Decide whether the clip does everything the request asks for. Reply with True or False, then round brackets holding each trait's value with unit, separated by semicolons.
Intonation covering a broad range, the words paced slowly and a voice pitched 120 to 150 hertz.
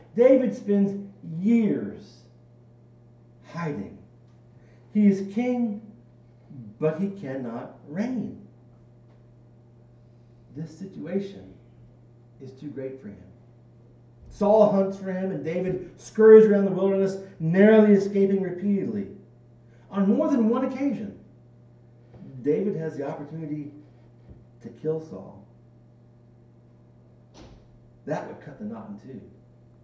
True (8.8 semitones; 100 wpm; 135 Hz)